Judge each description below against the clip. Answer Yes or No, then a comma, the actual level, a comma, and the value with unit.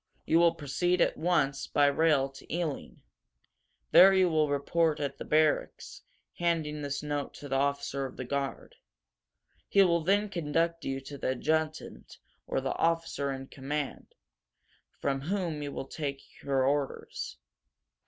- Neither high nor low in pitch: Yes, medium, 150 Hz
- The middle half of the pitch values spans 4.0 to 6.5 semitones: No, average, 3.2 semitones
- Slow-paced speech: No, average, 155 wpm